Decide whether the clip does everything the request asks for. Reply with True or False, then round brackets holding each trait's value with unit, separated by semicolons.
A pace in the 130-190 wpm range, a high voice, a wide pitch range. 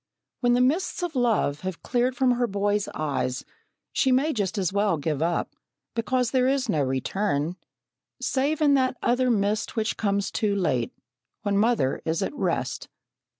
True (165 wpm; 215 Hz; 5.9 semitones)